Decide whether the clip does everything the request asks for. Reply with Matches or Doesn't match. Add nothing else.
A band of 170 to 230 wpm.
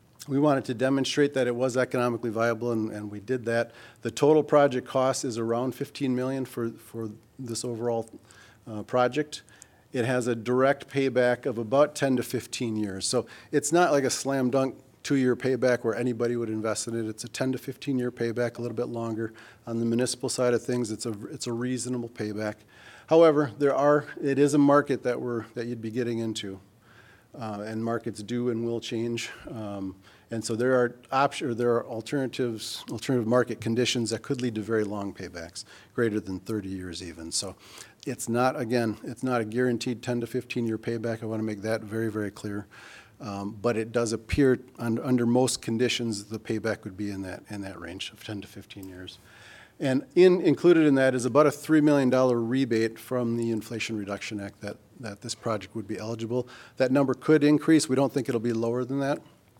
Matches